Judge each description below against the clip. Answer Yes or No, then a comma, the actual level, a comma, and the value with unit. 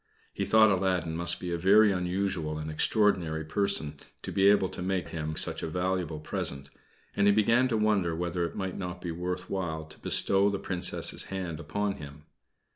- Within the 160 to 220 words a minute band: Yes, average, 190 wpm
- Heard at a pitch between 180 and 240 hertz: No, very low, 90 Hz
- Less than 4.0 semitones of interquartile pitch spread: Yes, average, 3.6 semitones